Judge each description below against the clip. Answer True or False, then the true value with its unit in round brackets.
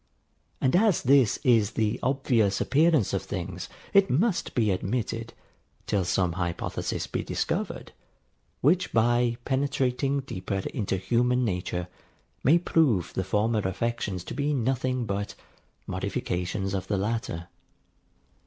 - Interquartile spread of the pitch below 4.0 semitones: False (5.5 semitones)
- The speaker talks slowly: True (125 wpm)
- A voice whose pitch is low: True (115 Hz)